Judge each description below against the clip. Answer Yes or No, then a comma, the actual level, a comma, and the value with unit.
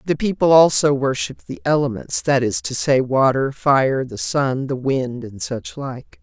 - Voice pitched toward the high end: No, low, 135 Hz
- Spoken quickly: No, average, 175 wpm